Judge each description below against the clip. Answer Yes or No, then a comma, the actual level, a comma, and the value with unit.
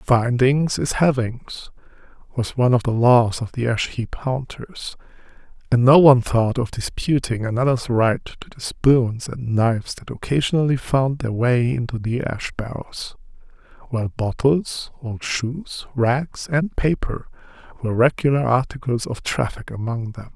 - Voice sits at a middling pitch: No, low, 125 Hz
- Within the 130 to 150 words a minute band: Yes, average, 145 wpm